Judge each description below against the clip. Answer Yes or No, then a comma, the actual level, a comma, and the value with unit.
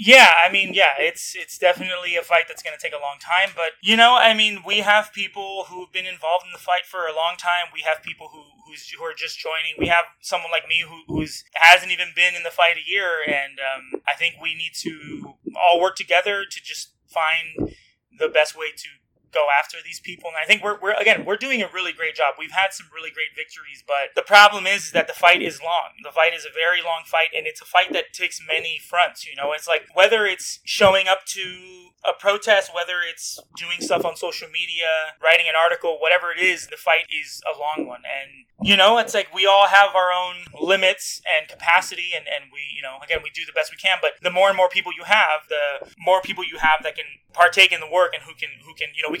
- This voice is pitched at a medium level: Yes, medium, 180 Hz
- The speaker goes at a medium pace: No, fast, 250 wpm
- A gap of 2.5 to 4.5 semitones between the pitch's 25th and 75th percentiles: Yes, average, 3.2 semitones